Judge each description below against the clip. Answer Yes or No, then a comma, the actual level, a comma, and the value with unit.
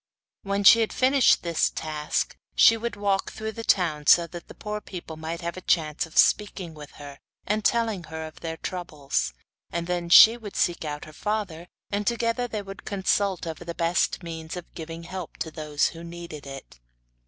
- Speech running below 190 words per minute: No, average, 200 wpm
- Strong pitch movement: No, average, 4.3 semitones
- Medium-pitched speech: Yes, medium, 170 Hz